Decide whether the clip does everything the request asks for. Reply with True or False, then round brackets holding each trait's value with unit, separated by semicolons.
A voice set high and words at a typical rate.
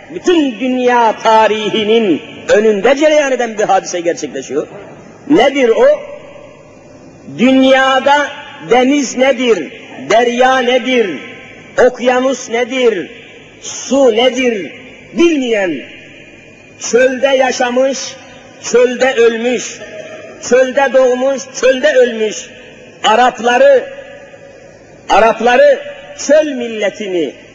False (255 Hz; 75 wpm)